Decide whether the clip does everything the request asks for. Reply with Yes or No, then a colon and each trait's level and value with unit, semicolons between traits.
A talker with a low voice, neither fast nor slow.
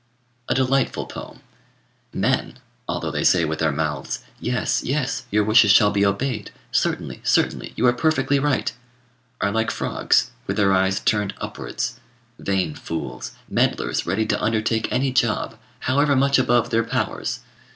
Yes: low, 110 Hz; average, 150 wpm